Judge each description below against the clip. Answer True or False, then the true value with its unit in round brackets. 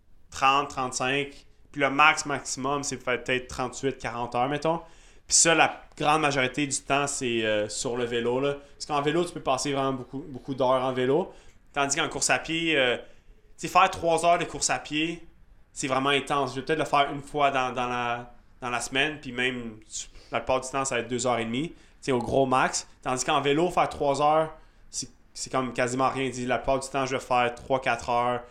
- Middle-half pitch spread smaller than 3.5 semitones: True (2.5 semitones)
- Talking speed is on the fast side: True (225 wpm)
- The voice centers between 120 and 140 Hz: True (135 Hz)